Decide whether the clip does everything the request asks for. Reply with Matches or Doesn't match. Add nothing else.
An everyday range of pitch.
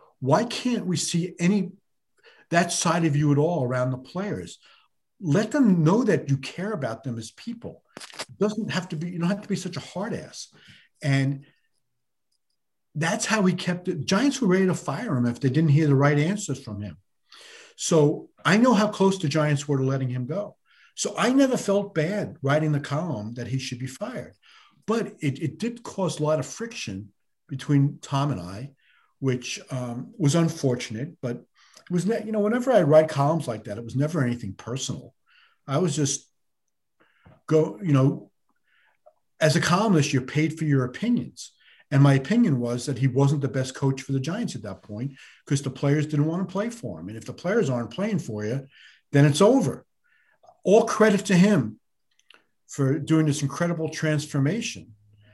Doesn't match